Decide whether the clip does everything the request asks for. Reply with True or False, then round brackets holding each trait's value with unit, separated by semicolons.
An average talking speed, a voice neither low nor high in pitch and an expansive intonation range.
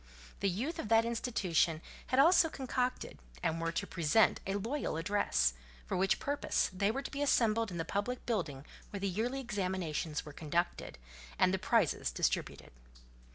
False (165 wpm; 200 Hz; 6.3 semitones)